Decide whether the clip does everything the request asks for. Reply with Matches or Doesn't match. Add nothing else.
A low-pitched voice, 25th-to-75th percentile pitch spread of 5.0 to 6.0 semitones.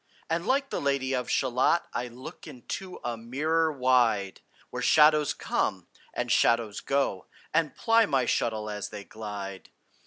Matches